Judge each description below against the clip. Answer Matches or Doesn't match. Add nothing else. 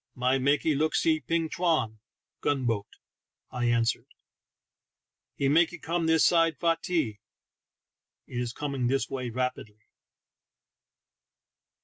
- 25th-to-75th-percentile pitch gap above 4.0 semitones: Matches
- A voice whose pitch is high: Doesn't match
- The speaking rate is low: Matches